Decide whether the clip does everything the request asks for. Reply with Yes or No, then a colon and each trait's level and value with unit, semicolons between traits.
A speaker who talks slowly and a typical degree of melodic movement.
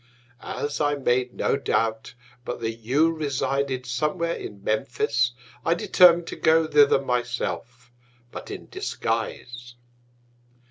Yes: slow, 125 wpm; average, 3.6 semitones